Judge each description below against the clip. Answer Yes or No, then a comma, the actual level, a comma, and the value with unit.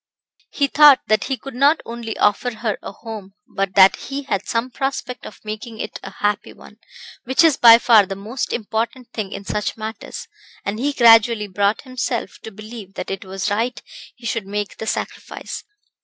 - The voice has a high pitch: Yes, high, 225 Hz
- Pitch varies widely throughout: No, average, 3.2 semitones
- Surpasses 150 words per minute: Yes, average, 185 wpm